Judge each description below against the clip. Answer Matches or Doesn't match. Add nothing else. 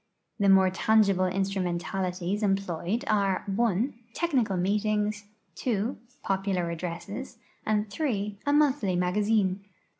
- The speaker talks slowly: Matches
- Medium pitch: Doesn't match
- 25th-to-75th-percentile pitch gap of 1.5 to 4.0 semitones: Matches